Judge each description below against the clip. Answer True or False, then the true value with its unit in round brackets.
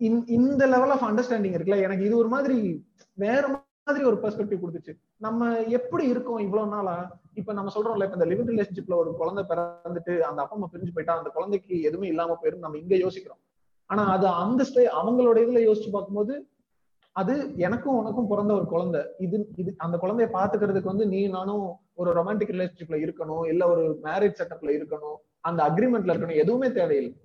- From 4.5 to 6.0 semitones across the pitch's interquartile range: True (5.0 semitones)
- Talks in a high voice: True (200 Hz)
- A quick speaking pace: True (165 wpm)